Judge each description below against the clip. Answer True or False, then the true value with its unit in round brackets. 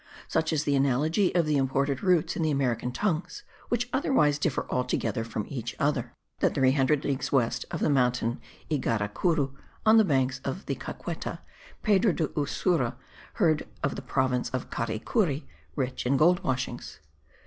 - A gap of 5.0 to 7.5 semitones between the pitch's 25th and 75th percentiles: False (4.3 semitones)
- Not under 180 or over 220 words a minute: False (160 wpm)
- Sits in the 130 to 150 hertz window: True (140 Hz)